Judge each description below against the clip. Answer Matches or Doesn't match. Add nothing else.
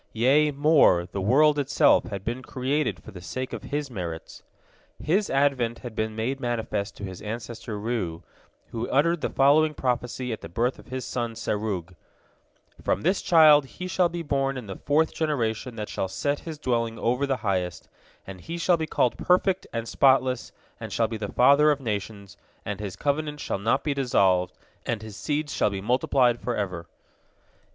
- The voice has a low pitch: Matches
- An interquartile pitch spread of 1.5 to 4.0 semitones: Doesn't match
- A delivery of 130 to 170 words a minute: Doesn't match